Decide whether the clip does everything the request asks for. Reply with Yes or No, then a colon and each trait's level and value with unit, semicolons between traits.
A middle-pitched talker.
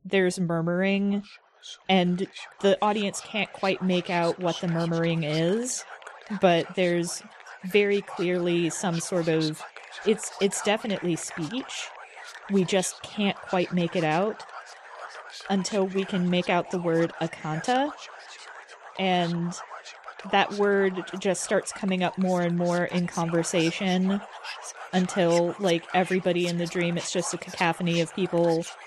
Yes: medium, 180 Hz